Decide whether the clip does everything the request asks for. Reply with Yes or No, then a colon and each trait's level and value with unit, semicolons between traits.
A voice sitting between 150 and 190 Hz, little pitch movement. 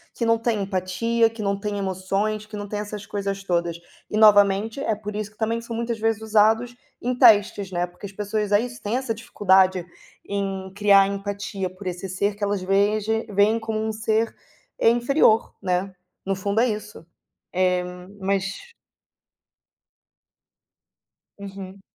No: high, 205 Hz; narrow, 2.1 semitones